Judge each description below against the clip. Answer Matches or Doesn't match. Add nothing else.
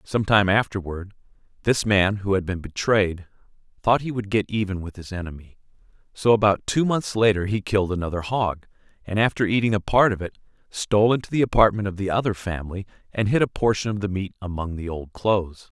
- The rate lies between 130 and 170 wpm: Doesn't match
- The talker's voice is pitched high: Doesn't match